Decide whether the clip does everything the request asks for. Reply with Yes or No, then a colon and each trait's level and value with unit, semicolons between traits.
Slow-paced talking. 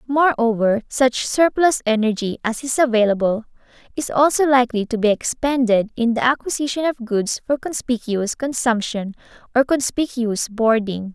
Yes: slow, 130 wpm